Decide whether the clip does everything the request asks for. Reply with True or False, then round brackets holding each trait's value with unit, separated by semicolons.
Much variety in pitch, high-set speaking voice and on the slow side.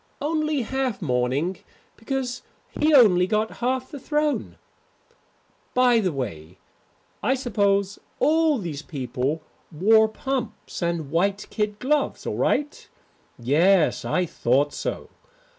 True (8.4 semitones; 210 Hz; 115 wpm)